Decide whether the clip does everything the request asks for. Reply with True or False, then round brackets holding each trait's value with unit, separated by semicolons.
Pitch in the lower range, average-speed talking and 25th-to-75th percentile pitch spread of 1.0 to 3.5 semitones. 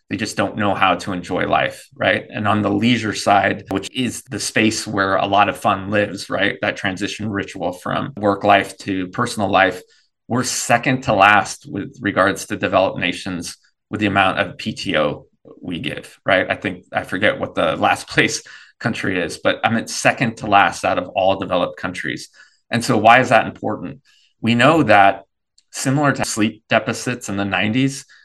True (105 Hz; 185 wpm; 3.1 semitones)